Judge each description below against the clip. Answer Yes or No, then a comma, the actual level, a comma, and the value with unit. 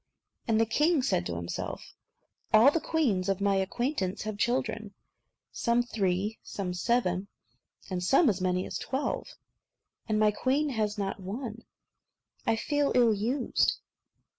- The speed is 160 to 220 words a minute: No, average, 140 wpm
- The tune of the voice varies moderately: Yes, average, 4.4 semitones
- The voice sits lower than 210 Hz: No, high, 215 Hz